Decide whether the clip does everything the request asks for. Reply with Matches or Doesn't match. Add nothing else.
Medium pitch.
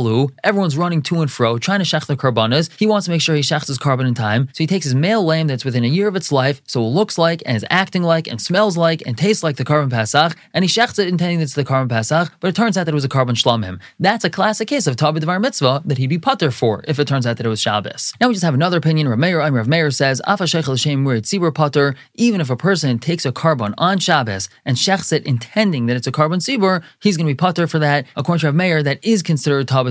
Matches